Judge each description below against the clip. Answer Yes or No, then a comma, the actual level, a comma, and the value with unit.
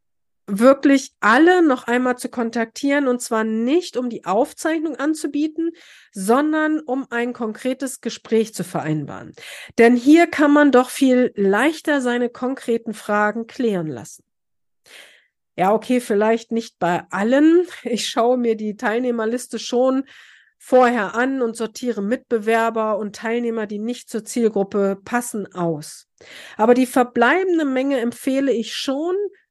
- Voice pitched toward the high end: Yes, high, 240 Hz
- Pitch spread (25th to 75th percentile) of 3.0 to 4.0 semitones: Yes, average, 3.4 semitones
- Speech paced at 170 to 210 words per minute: No, average, 130 wpm